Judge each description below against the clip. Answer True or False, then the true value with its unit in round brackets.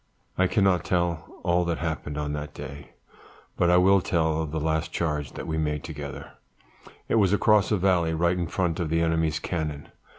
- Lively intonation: False (2.8 semitones)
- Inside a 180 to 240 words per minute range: True (195 wpm)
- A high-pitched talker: False (80 Hz)